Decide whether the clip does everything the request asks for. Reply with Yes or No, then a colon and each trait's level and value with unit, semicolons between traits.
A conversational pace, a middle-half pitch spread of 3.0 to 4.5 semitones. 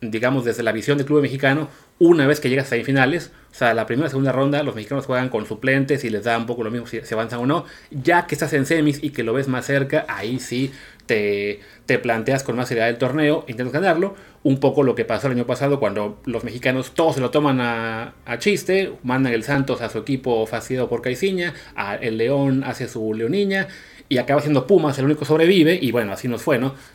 No: fast, 235 wpm; average, 3.5 semitones